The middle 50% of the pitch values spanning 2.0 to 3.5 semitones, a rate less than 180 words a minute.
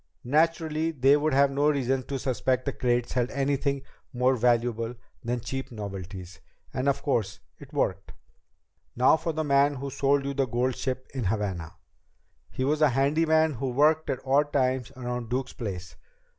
Yes: average, 2.7 semitones; average, 170 wpm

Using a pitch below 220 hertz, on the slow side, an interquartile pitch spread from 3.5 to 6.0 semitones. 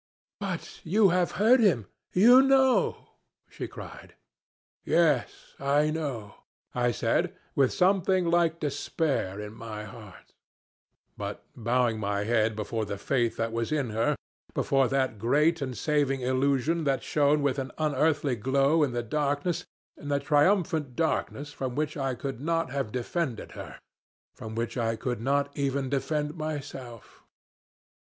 No: medium, 140 Hz; average, 145 wpm; average, 4.6 semitones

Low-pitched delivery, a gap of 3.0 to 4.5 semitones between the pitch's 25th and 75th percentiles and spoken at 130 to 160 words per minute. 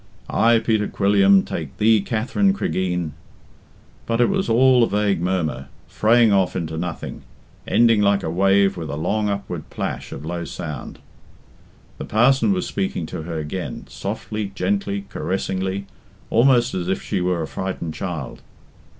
Yes: low, 100 Hz; average, 4.2 semitones; average, 155 wpm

